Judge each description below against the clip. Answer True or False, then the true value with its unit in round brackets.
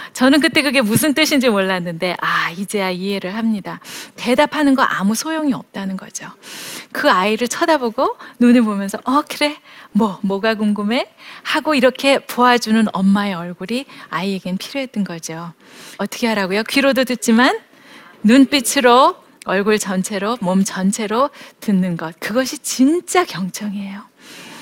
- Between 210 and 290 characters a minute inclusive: False (305 characters per minute)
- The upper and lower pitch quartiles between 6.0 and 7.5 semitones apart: False (5.6 semitones)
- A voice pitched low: False (225 Hz)